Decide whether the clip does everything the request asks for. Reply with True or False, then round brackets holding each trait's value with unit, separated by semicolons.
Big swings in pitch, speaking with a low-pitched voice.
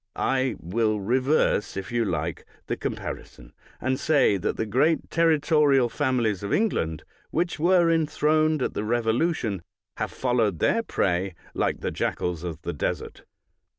True (7.7 semitones; 120 Hz)